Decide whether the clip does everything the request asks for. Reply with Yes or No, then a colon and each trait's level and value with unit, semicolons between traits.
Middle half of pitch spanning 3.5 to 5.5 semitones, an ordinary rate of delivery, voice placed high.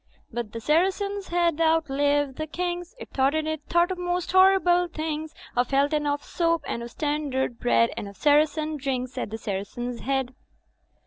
Yes: average, 4.7 semitones; average, 185 wpm; very high, 300 Hz